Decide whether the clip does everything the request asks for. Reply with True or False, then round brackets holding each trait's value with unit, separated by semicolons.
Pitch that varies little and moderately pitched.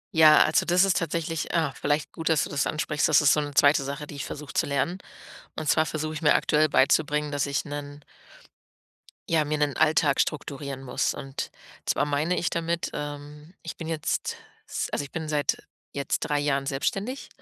True (1.9 semitones; 150 Hz)